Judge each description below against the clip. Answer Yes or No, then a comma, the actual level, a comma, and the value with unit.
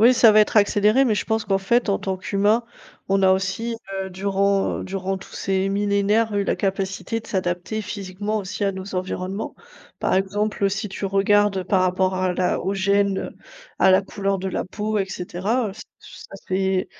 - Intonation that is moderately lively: No, narrow, 1.6 semitones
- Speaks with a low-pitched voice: No, high, 195 Hz